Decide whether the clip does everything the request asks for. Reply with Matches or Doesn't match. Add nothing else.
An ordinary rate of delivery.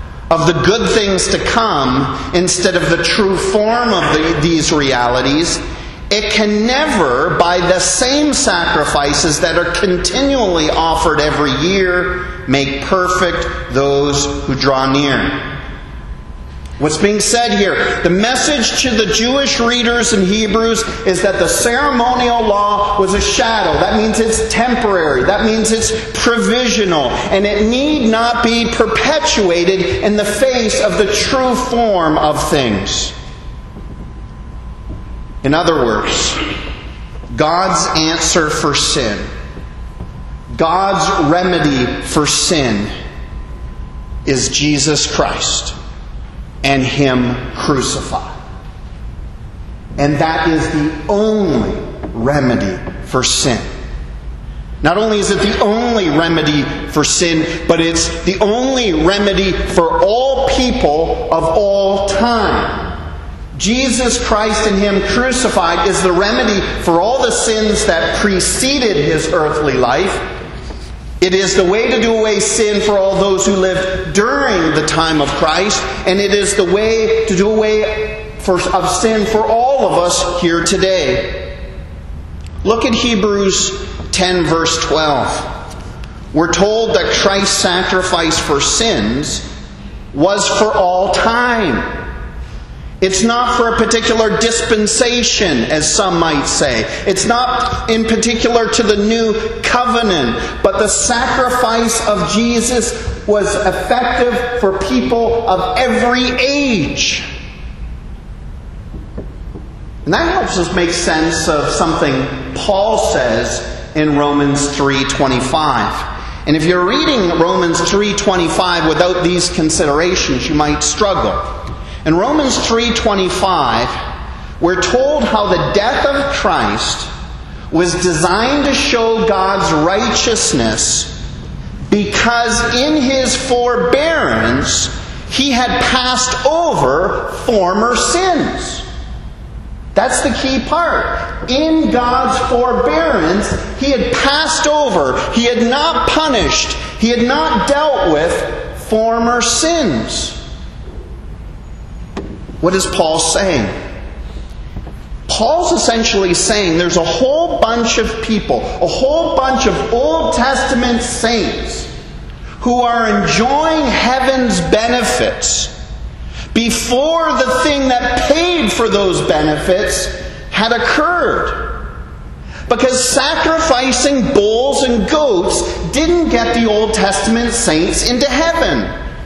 Doesn't match